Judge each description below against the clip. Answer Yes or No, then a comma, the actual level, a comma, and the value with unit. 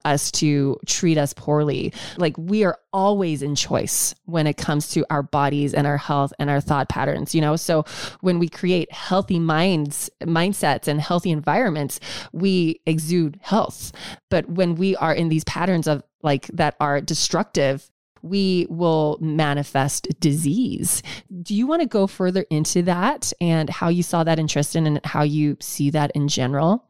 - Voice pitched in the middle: Yes, medium, 160 Hz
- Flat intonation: No, average, 3.5 semitones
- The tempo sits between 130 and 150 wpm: No, average, 170 wpm